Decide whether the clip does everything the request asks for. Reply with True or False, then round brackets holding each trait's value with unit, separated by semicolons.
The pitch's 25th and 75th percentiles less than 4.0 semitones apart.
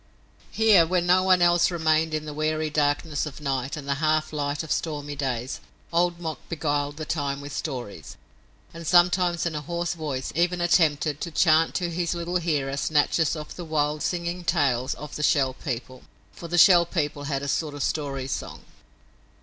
True (3.1 semitones)